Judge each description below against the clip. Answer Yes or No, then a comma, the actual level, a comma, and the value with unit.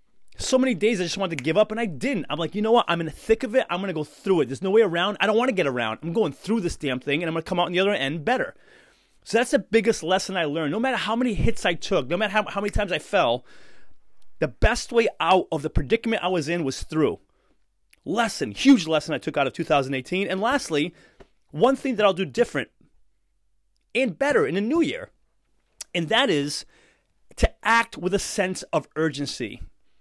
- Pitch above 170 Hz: Yes, high, 190 Hz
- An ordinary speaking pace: No, fast, 245 wpm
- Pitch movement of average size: No, wide, 6.0 semitones